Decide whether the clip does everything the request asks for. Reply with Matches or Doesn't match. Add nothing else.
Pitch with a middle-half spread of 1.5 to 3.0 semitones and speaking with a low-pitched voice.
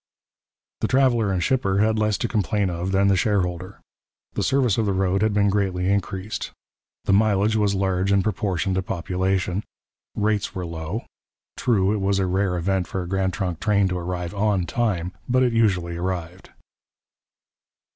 Matches